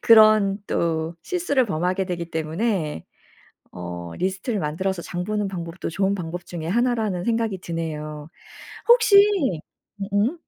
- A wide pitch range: No, average, 4.8 semitones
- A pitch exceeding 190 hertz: No, medium, 185 Hz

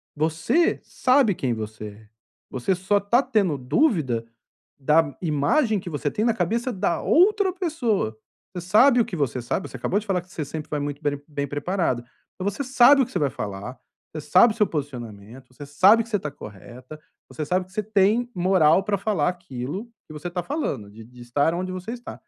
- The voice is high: No, medium, 175 Hz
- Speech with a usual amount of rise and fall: No, wide, 7.3 semitones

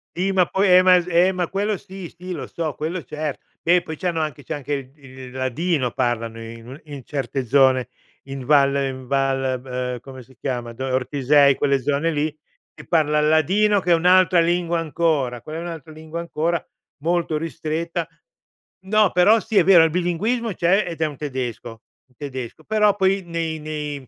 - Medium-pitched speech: Yes, medium, 155 Hz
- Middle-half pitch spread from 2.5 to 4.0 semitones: No, average, 4.8 semitones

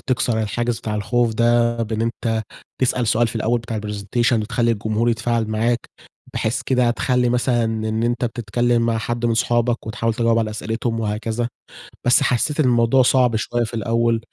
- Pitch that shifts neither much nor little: No, narrow, 1.4 semitones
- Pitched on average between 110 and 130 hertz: Yes, low, 115 Hz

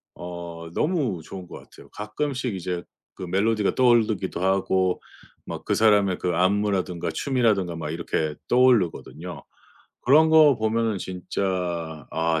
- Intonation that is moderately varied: Yes, average, 4.6 semitones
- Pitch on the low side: Yes, very low, 95 Hz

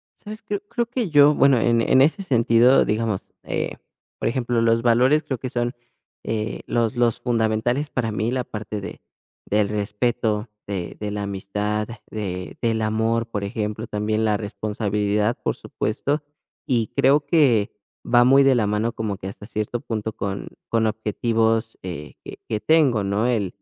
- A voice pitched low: Yes, low, 115 Hz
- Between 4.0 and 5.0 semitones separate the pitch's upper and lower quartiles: No, average, 2.7 semitones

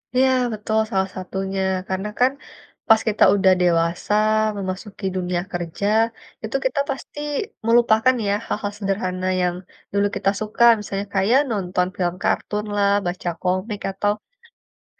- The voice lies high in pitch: Yes, high, 195 Hz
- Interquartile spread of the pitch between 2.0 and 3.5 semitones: Yes, average, 2.7 semitones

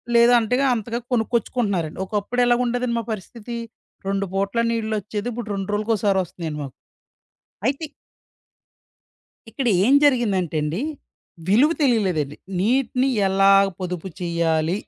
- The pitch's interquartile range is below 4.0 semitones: No, average, 4.4 semitones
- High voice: Yes, high, 210 Hz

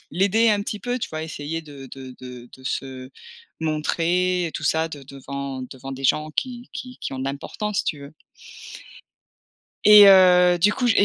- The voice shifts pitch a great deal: Yes, wide, 6.4 semitones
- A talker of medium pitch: Yes, medium, 160 Hz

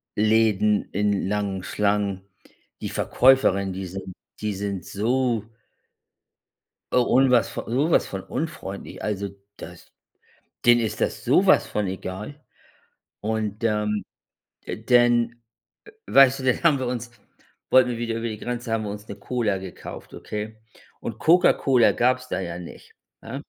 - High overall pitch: No, low, 110 Hz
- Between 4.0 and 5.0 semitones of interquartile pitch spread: No, average, 3.3 semitones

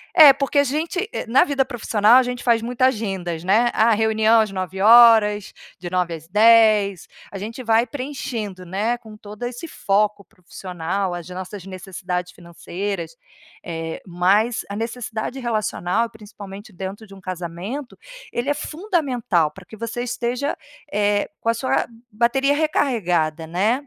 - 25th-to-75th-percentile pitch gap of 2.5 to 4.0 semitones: No, average, 4.5 semitones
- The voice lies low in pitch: No, high, 215 Hz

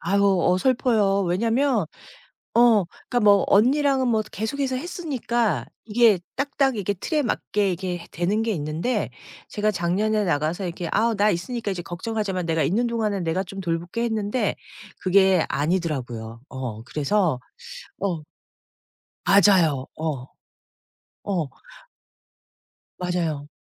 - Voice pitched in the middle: No, high, 195 Hz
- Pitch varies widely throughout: No, average, 5.0 semitones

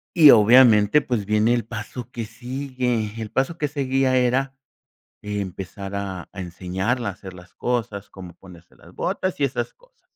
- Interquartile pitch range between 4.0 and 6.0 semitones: Yes, average, 4.7 semitones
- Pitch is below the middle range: Yes, low, 115 Hz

